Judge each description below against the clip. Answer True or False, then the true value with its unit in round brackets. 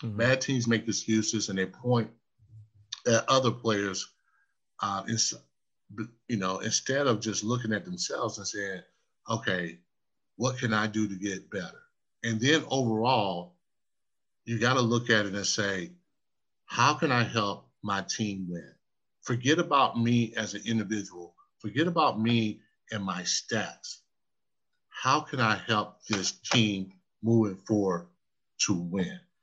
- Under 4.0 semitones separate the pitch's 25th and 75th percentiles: True (2.9 semitones)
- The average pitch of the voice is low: True (110 Hz)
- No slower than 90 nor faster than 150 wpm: True (145 wpm)